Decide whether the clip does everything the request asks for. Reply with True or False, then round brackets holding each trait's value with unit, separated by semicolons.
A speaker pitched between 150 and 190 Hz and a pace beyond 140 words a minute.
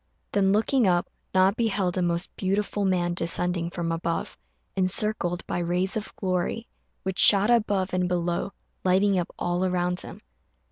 True (185 Hz; 155 wpm)